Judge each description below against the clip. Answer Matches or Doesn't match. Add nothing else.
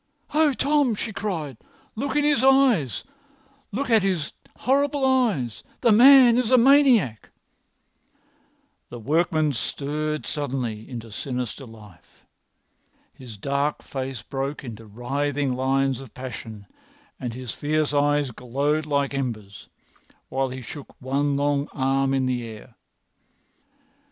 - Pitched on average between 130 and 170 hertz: Matches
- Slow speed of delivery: Matches